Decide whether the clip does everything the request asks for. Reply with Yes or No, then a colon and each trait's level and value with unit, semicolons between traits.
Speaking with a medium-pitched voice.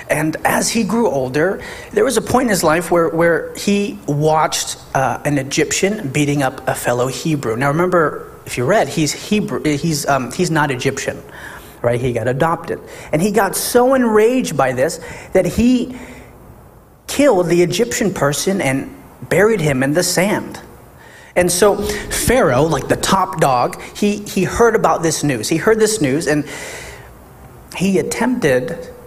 Yes: medium, 170 Hz